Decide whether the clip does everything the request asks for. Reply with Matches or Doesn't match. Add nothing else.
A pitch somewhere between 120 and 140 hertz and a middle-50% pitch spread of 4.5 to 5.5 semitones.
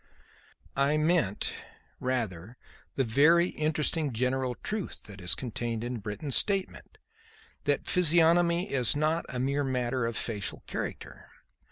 Matches